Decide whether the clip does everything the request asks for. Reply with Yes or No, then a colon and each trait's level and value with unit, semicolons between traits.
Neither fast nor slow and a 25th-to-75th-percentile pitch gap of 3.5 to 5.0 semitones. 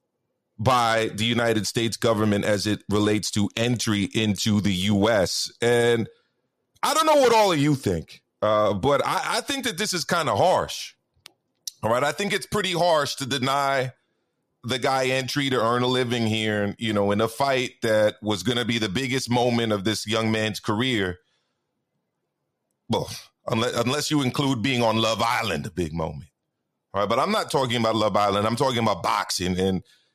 Yes: average, 190 wpm; average, 4.2 semitones